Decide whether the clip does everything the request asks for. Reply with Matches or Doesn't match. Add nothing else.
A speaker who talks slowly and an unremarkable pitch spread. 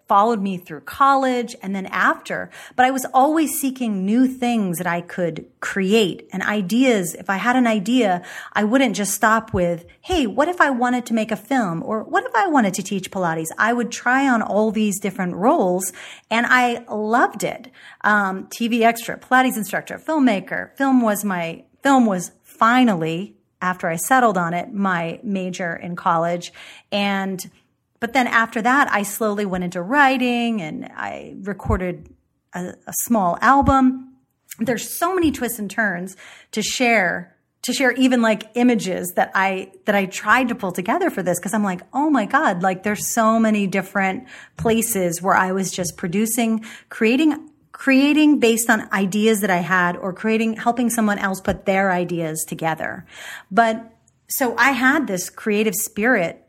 Doesn't match